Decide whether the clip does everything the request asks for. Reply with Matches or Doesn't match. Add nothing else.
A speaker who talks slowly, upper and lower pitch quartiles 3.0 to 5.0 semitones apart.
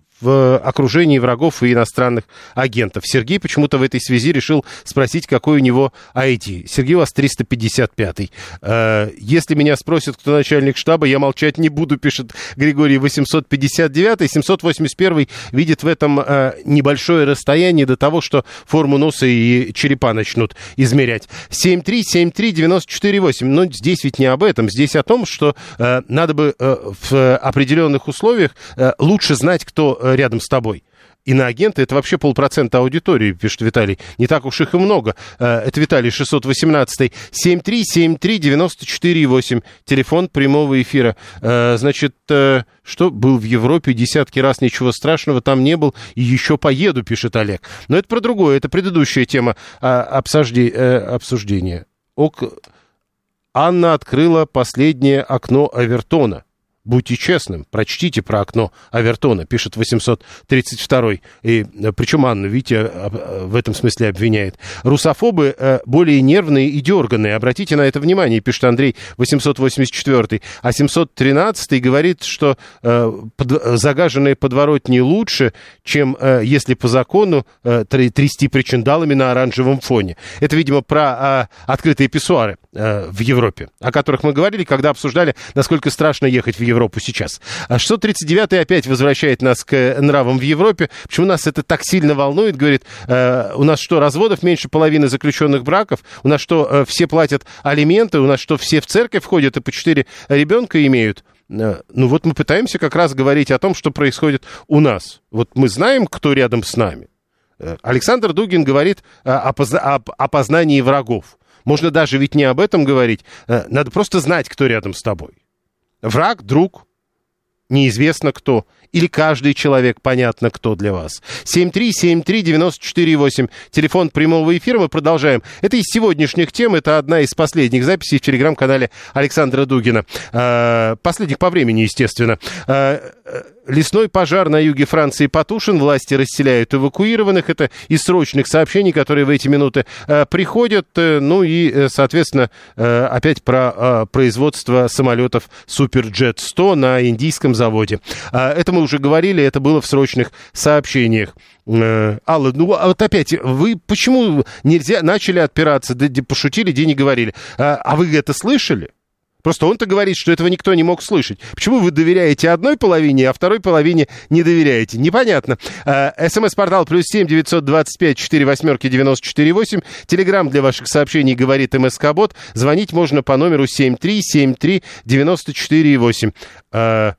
Doesn't match